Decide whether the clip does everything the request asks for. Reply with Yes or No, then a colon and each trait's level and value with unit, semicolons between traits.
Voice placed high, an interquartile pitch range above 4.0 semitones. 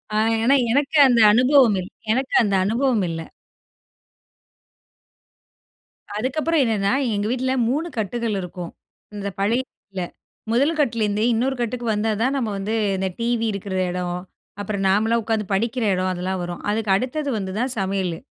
Yes: high, 220 Hz; average, 4.4 semitones